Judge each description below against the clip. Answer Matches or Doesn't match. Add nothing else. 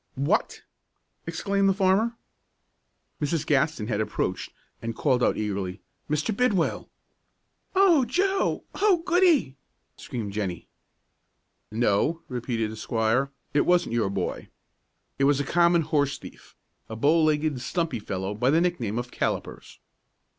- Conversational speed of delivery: Doesn't match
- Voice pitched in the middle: Matches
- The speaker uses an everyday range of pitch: Doesn't match